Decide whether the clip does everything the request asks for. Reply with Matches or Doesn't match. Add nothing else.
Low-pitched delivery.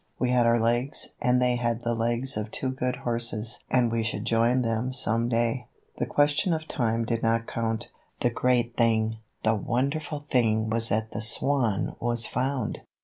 Matches